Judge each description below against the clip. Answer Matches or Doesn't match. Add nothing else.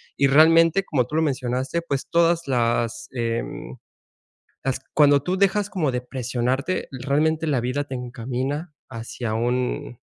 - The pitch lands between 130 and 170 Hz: Matches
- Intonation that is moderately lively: Matches